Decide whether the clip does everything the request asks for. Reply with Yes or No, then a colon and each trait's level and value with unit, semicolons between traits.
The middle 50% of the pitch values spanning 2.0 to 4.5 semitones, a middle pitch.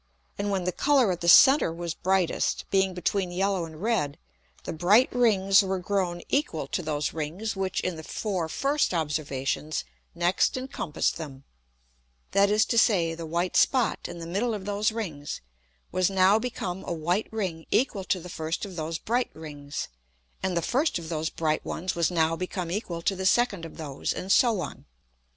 Yes: average, 3.8 semitones; medium, 180 Hz